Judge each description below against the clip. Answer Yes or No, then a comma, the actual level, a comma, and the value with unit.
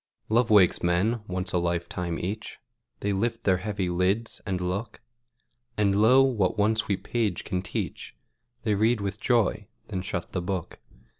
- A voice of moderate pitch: No, low, 100 Hz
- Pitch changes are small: No, average, 3.3 semitones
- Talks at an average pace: Yes, average, 160 wpm